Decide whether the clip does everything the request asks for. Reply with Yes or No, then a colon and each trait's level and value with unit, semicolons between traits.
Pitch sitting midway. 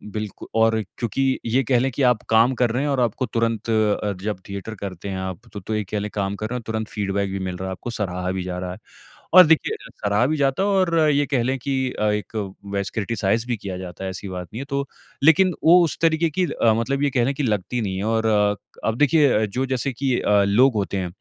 No: low, 115 Hz